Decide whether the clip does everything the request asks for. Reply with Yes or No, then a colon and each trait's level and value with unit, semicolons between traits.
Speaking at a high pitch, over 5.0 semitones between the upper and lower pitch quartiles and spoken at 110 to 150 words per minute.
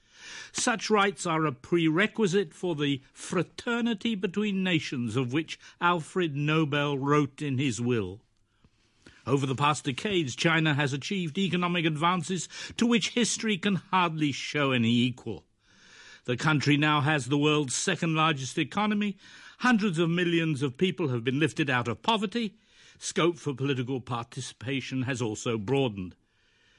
No: medium, 155 Hz; wide, 5.6 semitones; average, 140 wpm